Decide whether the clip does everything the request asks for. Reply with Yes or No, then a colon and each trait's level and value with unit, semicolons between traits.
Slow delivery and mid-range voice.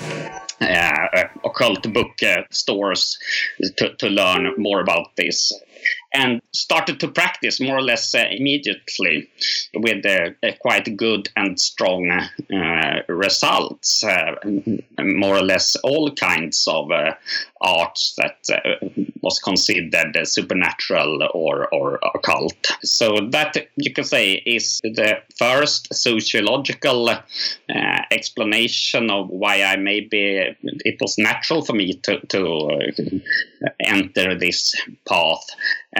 No: slow, 120 wpm; low, 120 Hz